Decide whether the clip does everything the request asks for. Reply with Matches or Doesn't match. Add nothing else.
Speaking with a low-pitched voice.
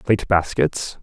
Matches